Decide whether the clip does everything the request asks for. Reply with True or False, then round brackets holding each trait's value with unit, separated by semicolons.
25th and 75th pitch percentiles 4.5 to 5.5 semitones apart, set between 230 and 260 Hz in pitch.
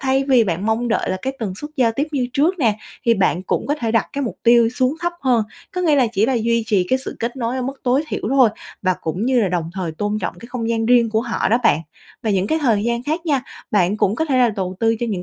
False (4.0 semitones; 235 Hz)